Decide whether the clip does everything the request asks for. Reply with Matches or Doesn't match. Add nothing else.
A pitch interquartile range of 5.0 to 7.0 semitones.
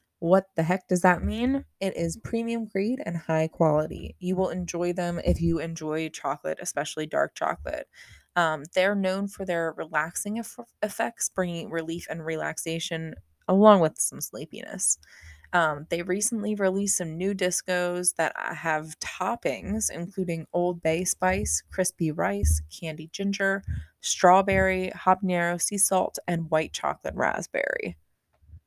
Doesn't match